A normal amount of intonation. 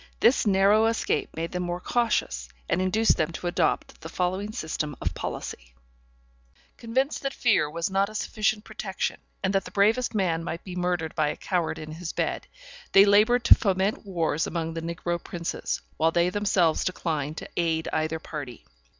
Yes: average, 4.1 semitones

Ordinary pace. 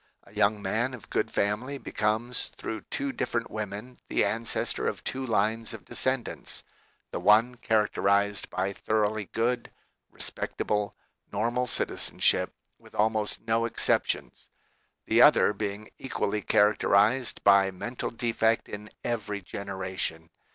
No: slow, 125 wpm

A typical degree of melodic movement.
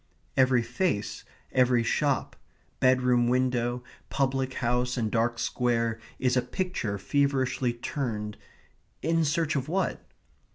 No: narrow, 2.3 semitones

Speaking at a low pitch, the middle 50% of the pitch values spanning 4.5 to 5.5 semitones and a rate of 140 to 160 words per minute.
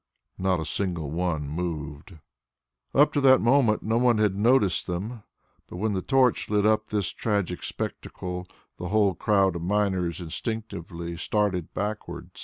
No: low, 100 Hz; average, 3.7 semitones; average, 150 wpm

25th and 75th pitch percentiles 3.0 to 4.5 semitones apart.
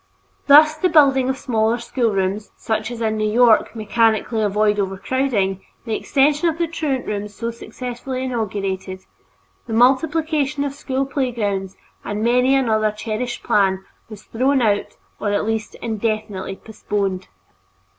Yes: average, 4.1 semitones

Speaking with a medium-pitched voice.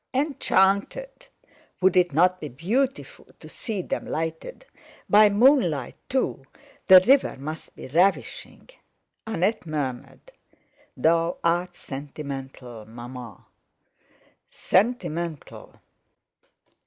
Yes: medium, 175 Hz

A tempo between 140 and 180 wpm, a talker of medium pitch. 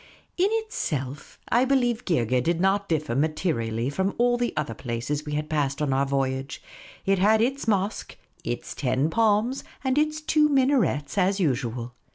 Yes: average, 170 wpm; medium, 165 Hz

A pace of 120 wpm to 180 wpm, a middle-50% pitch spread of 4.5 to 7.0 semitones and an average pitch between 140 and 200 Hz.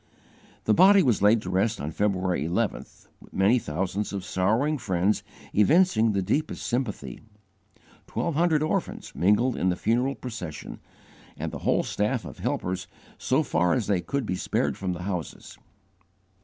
No: average, 155 wpm; wide, 5.5 semitones; low, 105 Hz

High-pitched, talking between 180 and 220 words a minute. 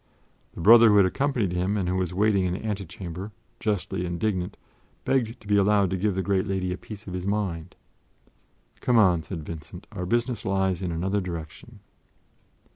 No: very low, 95 Hz; average, 185 wpm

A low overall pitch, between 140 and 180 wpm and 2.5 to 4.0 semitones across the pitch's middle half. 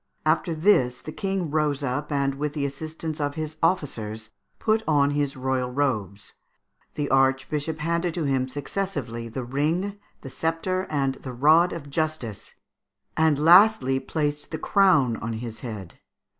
No: medium, 145 Hz; average, 150 wpm; average, 3.5 semitones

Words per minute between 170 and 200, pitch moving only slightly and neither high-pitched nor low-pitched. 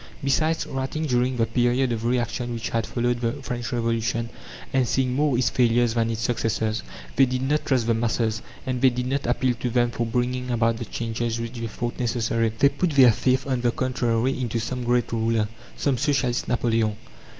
No: average, 195 wpm; narrow, 1.9 semitones; low, 120 Hz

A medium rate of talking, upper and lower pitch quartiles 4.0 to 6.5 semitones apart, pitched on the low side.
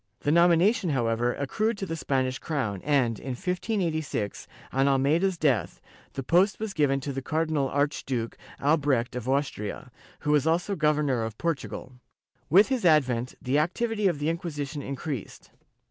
No: average, 160 wpm; average, 4.3 semitones; medium, 145 Hz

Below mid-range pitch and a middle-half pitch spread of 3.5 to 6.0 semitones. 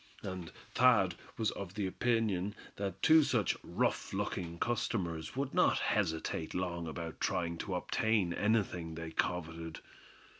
Yes: very low, 90 Hz; average, 4.5 semitones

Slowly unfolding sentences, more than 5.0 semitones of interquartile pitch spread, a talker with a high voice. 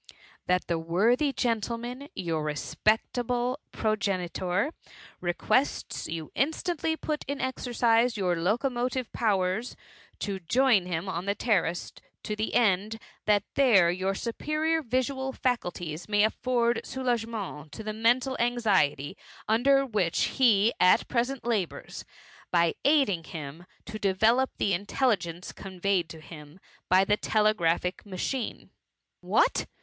Yes: slow, 130 wpm; wide, 5.4 semitones; high, 215 Hz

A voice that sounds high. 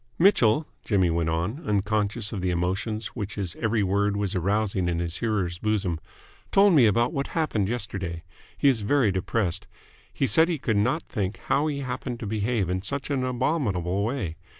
No: low, 105 Hz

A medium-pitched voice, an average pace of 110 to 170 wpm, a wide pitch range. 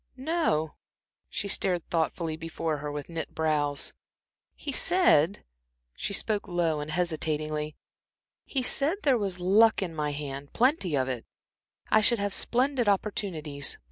Yes: medium, 170 Hz; average, 140 wpm; wide, 6.2 semitones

